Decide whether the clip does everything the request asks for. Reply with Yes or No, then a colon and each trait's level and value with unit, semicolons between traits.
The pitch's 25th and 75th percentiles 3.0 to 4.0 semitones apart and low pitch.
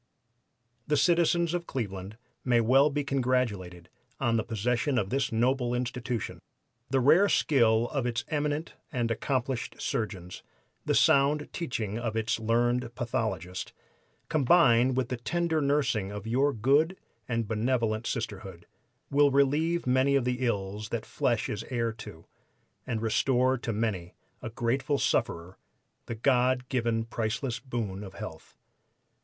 Yes: average, 3.6 semitones; low, 120 Hz